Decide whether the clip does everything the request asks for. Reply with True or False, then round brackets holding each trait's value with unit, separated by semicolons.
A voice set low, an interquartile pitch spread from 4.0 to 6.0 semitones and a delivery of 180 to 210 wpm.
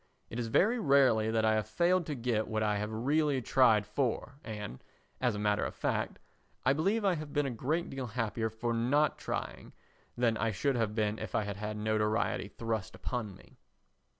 True (115 Hz; 4.3 semitones; 200 wpm)